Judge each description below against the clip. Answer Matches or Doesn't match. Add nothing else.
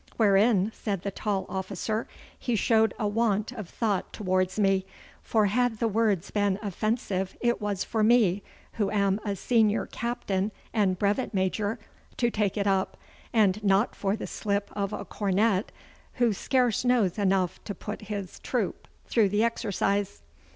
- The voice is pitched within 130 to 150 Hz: Doesn't match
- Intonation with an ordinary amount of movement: Doesn't match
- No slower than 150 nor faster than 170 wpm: Matches